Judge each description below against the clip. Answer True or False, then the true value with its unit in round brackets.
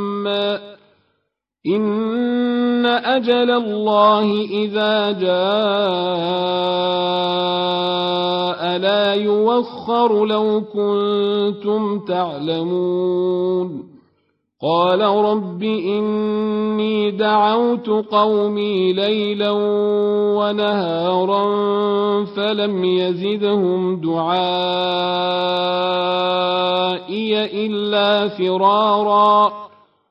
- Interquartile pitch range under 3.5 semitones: True (2.6 semitones)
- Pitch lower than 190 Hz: False (205 Hz)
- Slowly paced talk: True (45 wpm)